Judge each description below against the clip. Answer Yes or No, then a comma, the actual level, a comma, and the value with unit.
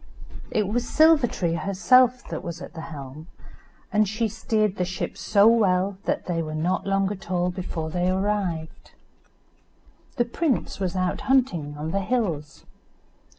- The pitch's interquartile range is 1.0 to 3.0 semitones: No, average, 4.2 semitones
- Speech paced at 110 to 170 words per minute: Yes, average, 155 wpm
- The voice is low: No, high, 190 Hz